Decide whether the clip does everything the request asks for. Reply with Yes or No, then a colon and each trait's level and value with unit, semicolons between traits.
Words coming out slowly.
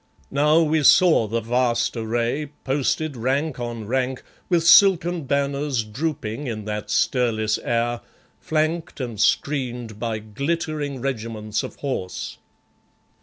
Yes: slow, 120 wpm